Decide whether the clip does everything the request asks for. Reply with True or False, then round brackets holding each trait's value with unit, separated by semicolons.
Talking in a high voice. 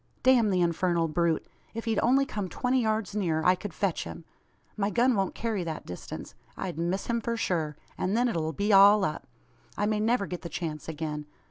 True (195 Hz)